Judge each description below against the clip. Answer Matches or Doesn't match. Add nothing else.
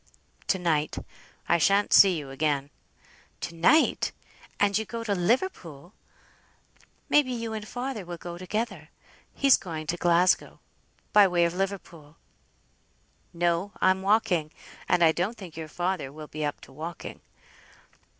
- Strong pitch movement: Doesn't match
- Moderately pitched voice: Matches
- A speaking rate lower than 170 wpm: Matches